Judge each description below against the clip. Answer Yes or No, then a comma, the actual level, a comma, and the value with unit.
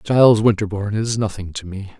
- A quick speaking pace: No, average, 180 wpm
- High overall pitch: No, low, 105 Hz